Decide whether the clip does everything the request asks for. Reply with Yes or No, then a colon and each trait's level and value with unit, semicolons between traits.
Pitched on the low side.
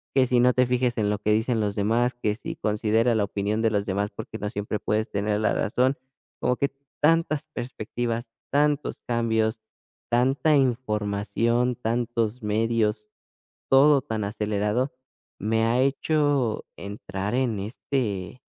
Yes: low, 115 Hz